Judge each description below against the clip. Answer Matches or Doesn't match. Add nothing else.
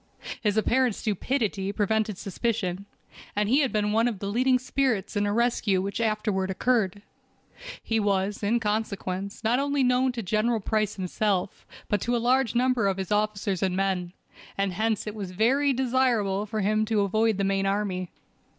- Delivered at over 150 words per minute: Matches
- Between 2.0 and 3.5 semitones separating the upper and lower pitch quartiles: Matches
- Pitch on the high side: Matches